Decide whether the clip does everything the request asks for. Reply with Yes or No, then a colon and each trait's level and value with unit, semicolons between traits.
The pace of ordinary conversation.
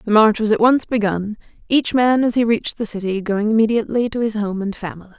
No: fast, 230 wpm